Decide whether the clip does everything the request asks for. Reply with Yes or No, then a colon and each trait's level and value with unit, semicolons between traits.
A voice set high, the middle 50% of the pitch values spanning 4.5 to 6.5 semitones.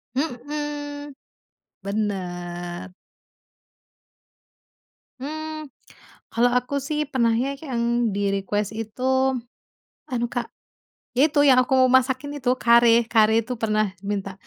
Yes: high, 240 Hz; average, 4.8 semitones